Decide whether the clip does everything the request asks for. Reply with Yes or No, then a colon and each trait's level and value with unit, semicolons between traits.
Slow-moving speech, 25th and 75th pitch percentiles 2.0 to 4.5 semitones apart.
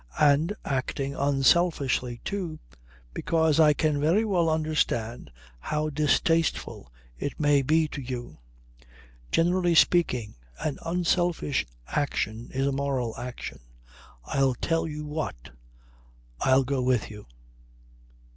Yes: slow, 110 wpm; average, 3.8 semitones